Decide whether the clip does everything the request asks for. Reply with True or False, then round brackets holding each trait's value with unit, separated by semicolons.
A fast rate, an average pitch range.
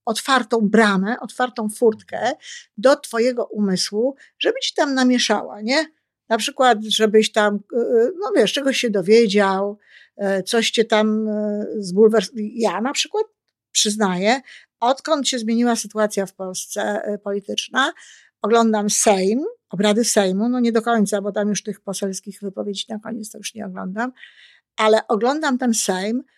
False (135 wpm; 3.1 semitones)